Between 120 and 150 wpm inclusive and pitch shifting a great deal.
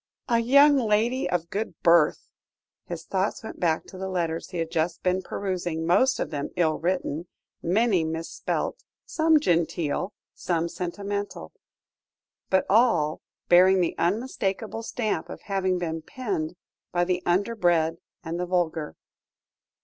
No: average, 140 wpm; average, 3.7 semitones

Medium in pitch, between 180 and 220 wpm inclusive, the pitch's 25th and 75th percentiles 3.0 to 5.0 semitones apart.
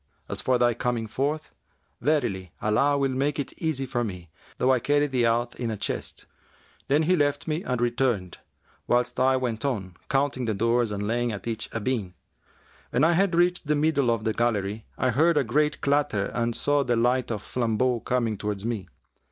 No: low, 125 Hz; average, 195 wpm; average, 4.1 semitones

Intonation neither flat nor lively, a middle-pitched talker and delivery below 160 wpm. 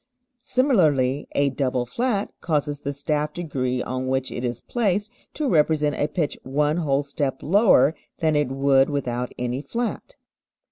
Yes: average, 4.1 semitones; medium, 145 Hz; average, 150 wpm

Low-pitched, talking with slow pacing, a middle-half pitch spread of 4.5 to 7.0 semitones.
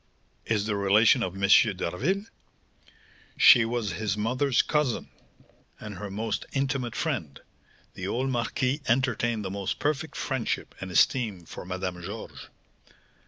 Yes: low, 110 Hz; slow, 130 wpm; average, 4.8 semitones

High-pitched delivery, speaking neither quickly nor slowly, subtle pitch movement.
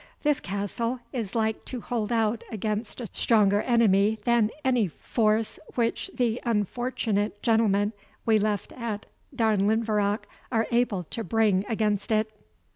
No: high, 220 Hz; slow, 130 wpm; narrow, 2.1 semitones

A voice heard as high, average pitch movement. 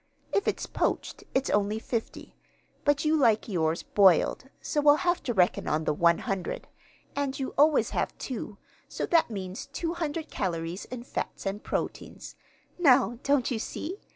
No: high, 240 Hz; wide, 7.0 semitones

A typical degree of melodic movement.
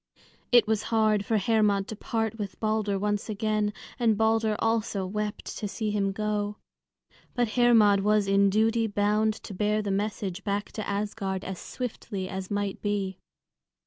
No: narrow, 1.6 semitones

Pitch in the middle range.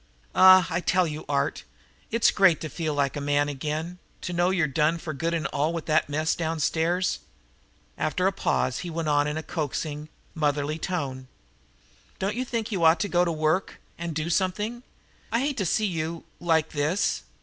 Yes: medium, 165 Hz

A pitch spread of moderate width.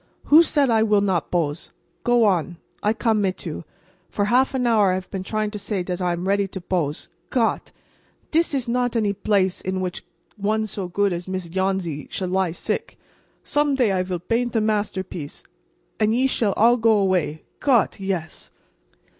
Yes: average, 3.6 semitones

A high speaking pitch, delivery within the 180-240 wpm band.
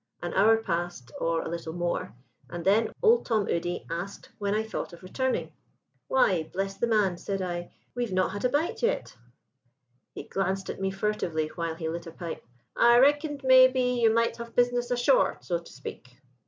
Yes: high, 195 Hz; average, 185 wpm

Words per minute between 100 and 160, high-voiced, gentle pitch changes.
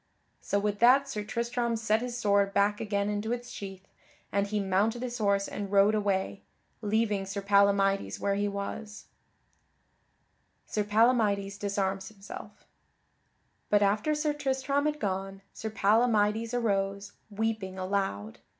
Yes: average, 140 wpm; high, 205 Hz; narrow, 2.3 semitones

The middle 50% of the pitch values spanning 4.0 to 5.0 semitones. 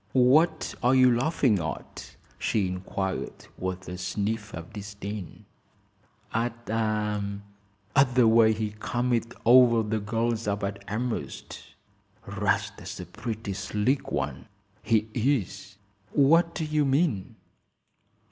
No: average, 3.5 semitones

